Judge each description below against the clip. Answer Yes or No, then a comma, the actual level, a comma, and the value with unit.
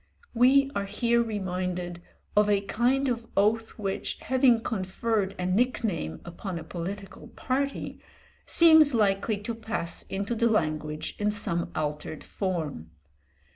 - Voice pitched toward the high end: Yes, high, 205 Hz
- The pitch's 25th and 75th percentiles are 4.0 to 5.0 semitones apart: Yes, average, 4.4 semitones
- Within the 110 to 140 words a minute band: Yes, slow, 135 wpm